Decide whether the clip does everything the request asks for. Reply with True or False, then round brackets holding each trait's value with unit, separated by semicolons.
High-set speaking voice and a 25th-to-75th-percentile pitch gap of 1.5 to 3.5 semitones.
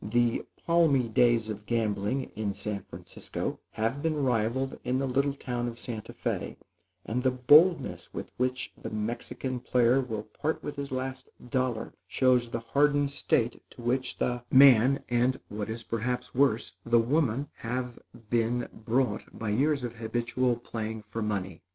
False (120 Hz; 2.6 semitones)